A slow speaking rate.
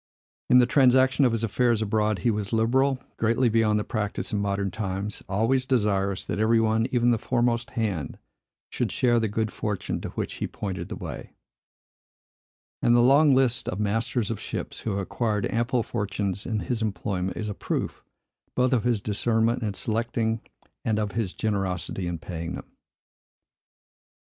No: average, 170 wpm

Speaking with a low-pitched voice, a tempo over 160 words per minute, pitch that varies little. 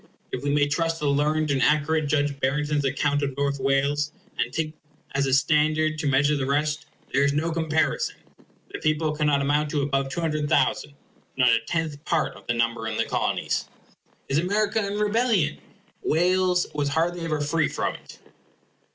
No: medium, 150 Hz; average, 175 wpm; narrow, 2.1 semitones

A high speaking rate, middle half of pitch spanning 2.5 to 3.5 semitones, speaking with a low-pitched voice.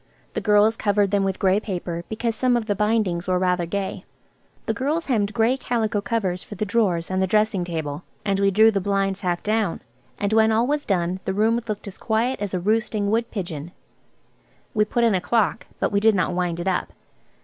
No: fast, 215 wpm; average, 3.1 semitones; high, 205 Hz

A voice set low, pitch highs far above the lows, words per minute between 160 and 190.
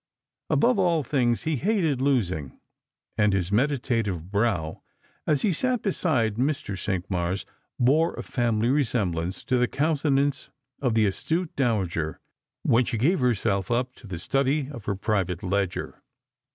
No: low, 120 Hz; wide, 6.5 semitones; average, 140 wpm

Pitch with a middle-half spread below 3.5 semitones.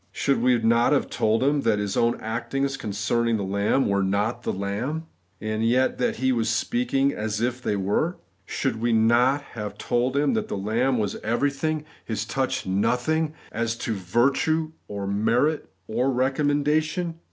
No: average, 4.2 semitones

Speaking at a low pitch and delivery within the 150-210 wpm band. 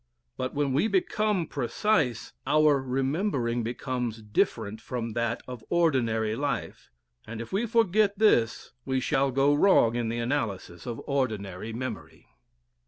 No: low, 130 Hz; slow, 135 wpm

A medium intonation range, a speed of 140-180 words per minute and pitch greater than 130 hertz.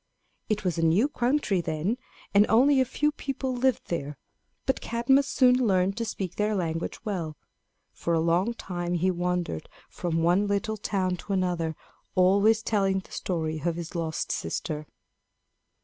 Yes: average, 4.7 semitones; average, 160 wpm; high, 190 Hz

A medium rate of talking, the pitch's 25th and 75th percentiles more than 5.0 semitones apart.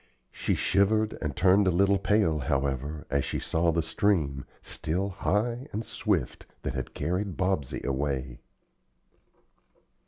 No: slow, 130 wpm; wide, 5.6 semitones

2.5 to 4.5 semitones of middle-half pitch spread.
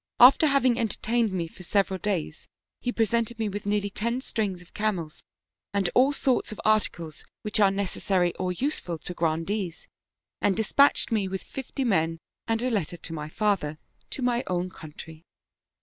No: average, 4.9 semitones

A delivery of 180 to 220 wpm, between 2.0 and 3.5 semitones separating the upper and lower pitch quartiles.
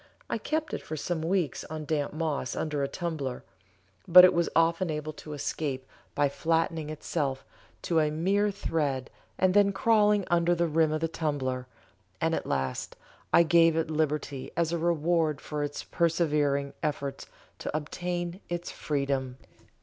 No: average, 160 wpm; average, 2.9 semitones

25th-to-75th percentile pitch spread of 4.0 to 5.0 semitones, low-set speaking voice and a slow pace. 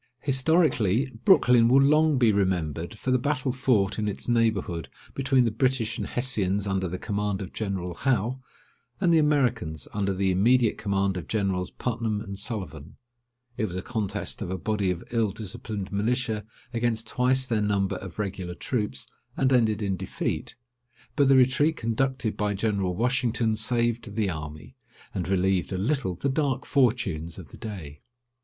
No: average, 4.7 semitones; low, 110 Hz; average, 165 wpm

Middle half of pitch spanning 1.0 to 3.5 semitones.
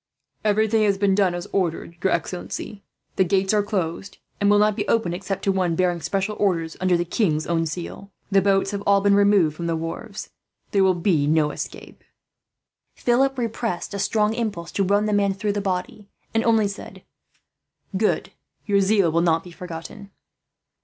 Yes: average, 3.0 semitones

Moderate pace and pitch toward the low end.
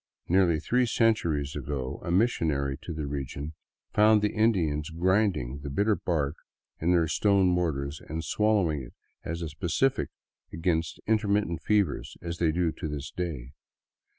Yes: average, 150 wpm; very low, 85 Hz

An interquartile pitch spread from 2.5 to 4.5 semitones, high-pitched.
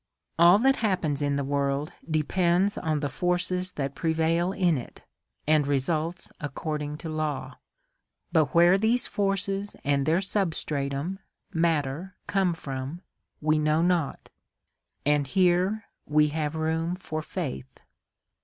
No: average, 3.7 semitones; medium, 160 Hz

